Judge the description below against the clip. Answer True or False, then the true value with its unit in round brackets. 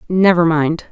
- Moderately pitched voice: True (170 Hz)